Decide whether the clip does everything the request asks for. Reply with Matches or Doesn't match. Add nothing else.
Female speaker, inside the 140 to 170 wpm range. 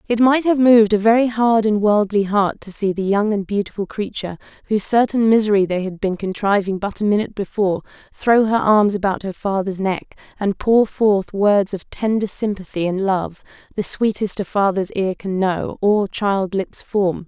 Doesn't match